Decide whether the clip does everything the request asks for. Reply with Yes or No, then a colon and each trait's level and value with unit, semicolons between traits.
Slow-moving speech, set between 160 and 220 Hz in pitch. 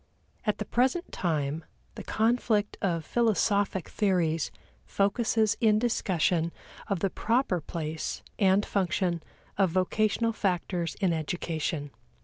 Yes: slow, 115 wpm; high, 190 Hz